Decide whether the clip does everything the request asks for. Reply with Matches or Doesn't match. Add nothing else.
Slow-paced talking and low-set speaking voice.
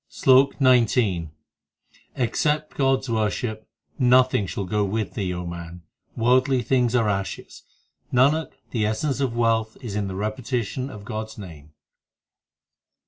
Matches